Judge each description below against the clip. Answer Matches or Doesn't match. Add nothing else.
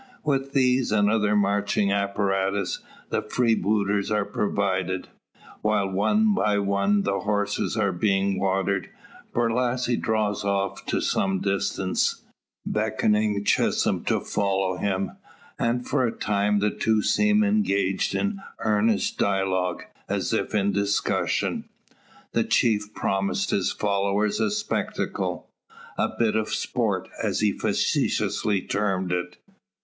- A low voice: Matches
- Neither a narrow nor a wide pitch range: Doesn't match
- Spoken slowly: Matches